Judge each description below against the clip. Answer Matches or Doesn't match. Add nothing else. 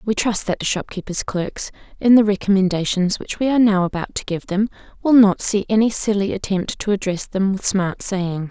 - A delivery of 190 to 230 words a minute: Matches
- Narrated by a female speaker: Matches